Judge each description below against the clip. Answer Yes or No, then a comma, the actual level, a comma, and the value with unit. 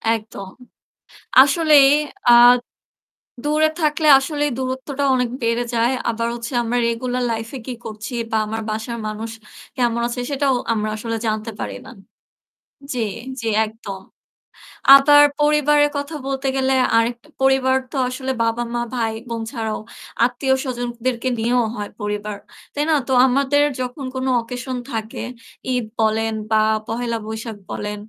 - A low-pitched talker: No, high, 245 Hz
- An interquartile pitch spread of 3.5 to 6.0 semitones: No, average, 3.1 semitones